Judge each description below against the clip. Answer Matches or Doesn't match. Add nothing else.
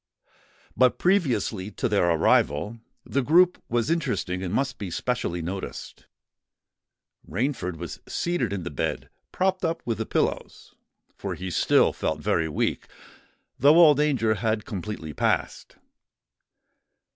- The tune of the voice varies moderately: Doesn't match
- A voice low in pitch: Matches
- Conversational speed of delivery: Doesn't match